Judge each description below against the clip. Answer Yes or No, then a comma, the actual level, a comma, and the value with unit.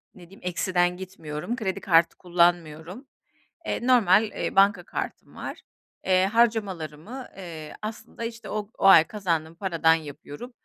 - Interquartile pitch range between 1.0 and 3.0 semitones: No, average, 4.2 semitones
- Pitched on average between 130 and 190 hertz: Yes, medium, 185 Hz